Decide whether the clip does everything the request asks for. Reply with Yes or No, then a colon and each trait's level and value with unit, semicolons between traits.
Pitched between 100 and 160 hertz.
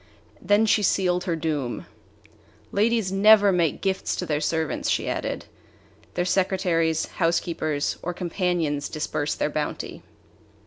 No: medium, 175 Hz